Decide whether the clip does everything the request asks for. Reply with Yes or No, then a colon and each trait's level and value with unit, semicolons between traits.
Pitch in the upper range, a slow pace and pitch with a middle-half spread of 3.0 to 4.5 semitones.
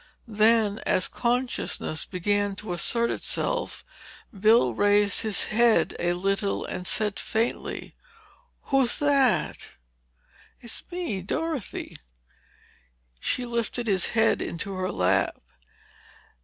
Yes: high, 215 Hz; slow, 100 wpm; average, 3.5 semitones